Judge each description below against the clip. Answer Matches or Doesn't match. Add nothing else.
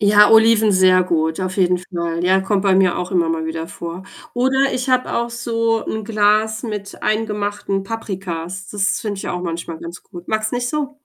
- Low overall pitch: Doesn't match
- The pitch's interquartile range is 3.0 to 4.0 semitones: Matches